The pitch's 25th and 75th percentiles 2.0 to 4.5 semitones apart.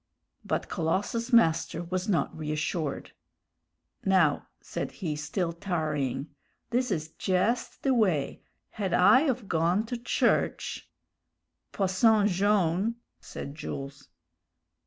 No: average, 5.0 semitones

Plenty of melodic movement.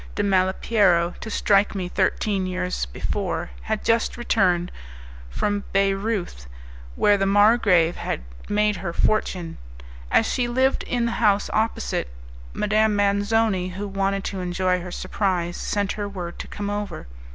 No: narrow, 2.5 semitones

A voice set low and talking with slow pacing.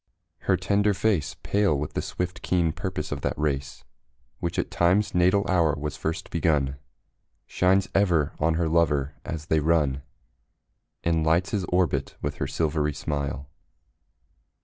No: very low, 80 Hz; average, 150 wpm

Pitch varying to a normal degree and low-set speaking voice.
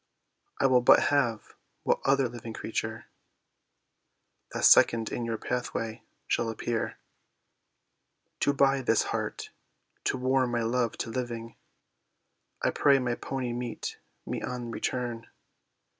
No: narrow, 2.0 semitones; low, 120 Hz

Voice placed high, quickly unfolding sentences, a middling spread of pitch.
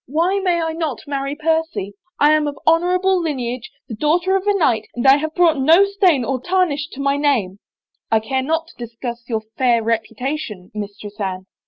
No: very high, 285 Hz; fast, 210 wpm; wide, 5.8 semitones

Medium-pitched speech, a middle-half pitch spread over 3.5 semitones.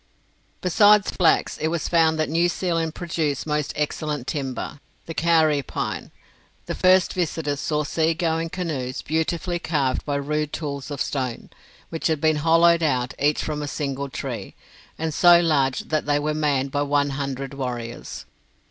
No: medium, 150 Hz; average, 2.7 semitones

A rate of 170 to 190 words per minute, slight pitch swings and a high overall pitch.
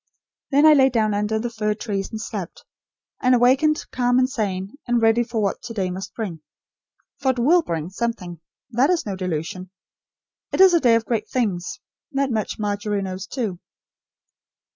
No: average, 180 wpm; average, 4.4 semitones; high, 220 Hz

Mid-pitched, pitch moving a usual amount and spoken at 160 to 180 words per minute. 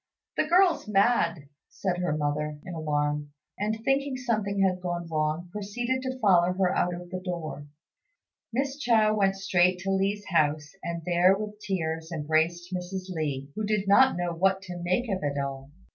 Yes: medium, 180 Hz; average, 4.4 semitones; average, 175 wpm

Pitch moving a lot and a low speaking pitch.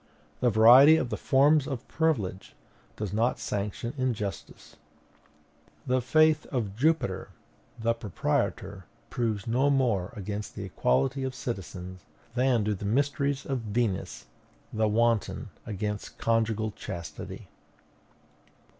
No: average, 4.3 semitones; low, 115 Hz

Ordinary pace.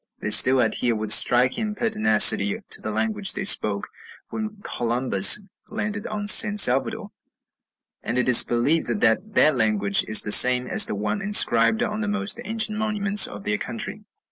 Yes: average, 165 wpm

